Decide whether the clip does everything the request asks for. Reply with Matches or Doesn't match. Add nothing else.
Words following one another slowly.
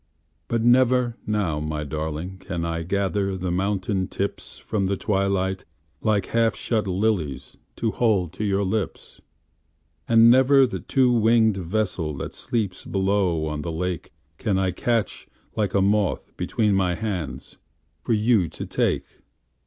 Matches